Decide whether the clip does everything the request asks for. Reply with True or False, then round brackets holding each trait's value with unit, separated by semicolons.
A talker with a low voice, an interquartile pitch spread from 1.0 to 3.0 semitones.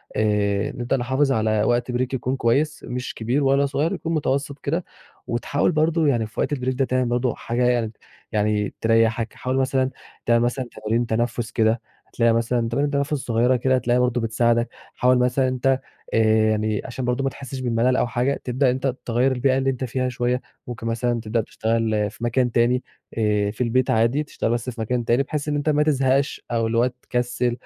True (125 Hz; 2.4 semitones)